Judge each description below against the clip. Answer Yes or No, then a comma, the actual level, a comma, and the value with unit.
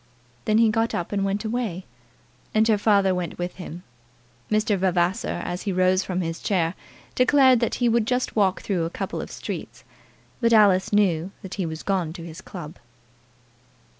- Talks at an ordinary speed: Yes, average, 180 wpm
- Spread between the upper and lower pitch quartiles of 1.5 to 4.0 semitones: Yes, average, 3.6 semitones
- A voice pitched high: Yes, high, 195 Hz